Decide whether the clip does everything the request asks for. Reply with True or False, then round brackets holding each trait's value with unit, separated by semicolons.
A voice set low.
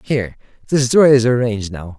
True (120 Hz)